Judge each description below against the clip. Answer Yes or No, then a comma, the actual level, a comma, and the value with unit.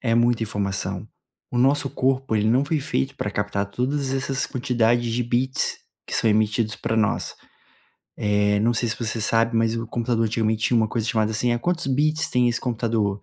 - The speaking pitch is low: Yes, low, 115 Hz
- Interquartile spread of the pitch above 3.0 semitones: No, narrow, 2.5 semitones